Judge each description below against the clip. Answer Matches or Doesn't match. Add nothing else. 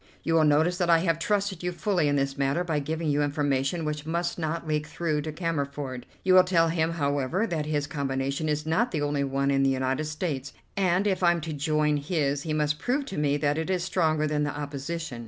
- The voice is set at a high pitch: Doesn't match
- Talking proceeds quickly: Matches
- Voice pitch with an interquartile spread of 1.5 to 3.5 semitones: Matches